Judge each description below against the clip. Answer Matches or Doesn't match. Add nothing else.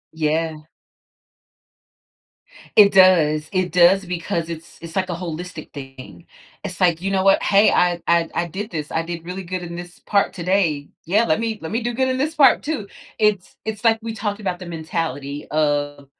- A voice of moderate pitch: Matches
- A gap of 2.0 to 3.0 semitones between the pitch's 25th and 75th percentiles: Doesn't match